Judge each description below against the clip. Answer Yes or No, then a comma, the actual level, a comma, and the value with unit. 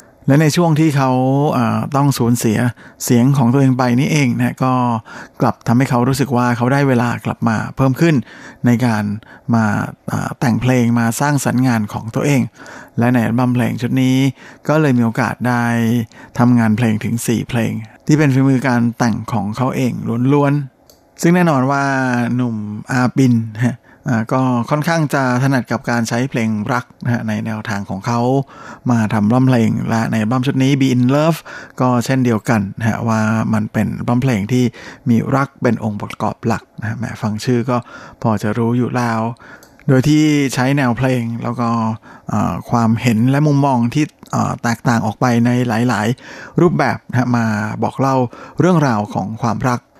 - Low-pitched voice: Yes, low, 120 Hz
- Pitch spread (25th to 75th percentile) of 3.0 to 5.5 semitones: No, narrow, 2.6 semitones